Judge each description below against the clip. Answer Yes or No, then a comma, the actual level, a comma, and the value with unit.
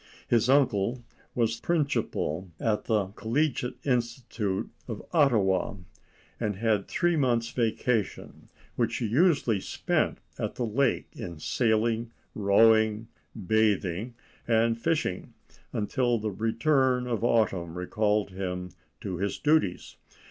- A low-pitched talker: Yes, low, 115 Hz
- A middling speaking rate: No, slow, 110 wpm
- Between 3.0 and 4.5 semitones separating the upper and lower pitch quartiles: Yes, average, 3.5 semitones